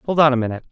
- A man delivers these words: Yes, male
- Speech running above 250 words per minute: Yes, fast, 335 wpm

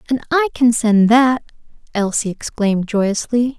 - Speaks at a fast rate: No, slow, 135 wpm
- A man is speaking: No, female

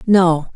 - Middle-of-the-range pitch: Yes, medium, 175 Hz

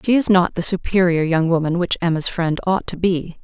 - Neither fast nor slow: No, fast, 225 wpm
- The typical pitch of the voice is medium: Yes, medium, 175 Hz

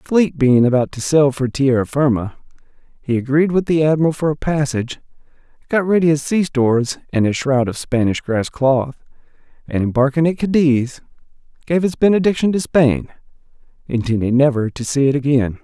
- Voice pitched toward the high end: No, medium, 140 Hz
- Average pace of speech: Yes, average, 165 wpm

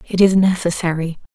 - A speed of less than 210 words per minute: Yes, slow, 135 wpm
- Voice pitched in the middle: Yes, medium, 175 Hz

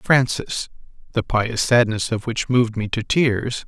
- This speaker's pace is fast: No, average, 165 wpm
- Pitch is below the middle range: Yes, low, 115 Hz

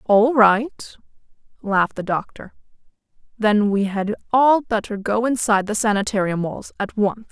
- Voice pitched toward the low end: No, high, 215 Hz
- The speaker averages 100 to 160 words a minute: Yes, average, 140 wpm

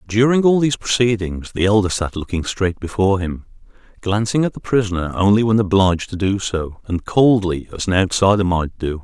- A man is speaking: Yes, male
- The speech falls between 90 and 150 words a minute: No, average, 185 wpm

